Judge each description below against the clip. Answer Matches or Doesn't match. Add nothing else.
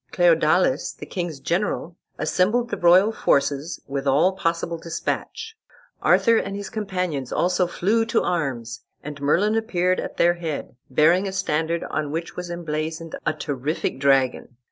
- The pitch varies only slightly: Doesn't match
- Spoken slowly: Doesn't match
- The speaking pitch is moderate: Matches